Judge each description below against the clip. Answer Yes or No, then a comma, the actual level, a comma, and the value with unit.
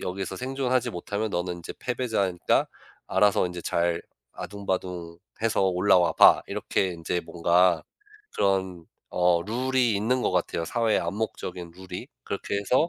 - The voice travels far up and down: No, average, 4.0 semitones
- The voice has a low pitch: Yes, very low, 95 Hz